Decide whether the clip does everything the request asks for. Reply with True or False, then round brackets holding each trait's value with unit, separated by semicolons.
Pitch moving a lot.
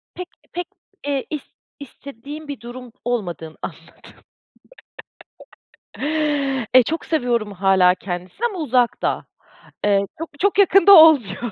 True (7.8 semitones)